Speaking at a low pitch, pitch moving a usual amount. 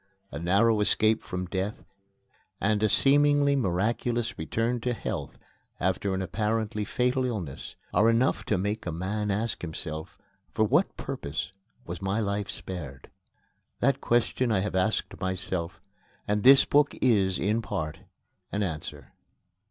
Yes: low, 105 Hz; average, 3.9 semitones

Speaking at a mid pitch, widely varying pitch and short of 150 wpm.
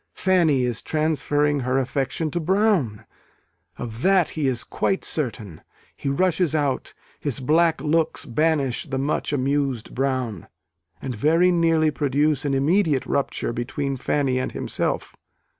No: medium, 145 Hz; average, 3.6 semitones; slow, 135 wpm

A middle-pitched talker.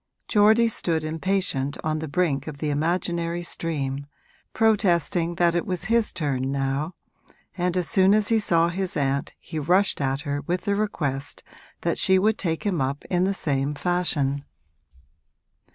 Yes: medium, 170 Hz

